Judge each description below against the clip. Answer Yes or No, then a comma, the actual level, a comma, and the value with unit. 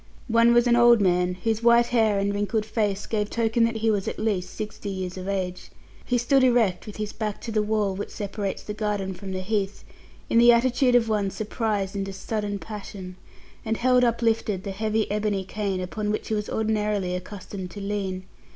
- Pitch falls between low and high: No, high, 210 Hz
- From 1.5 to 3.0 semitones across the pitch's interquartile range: Yes, narrow, 2.5 semitones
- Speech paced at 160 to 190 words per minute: No, average, 200 wpm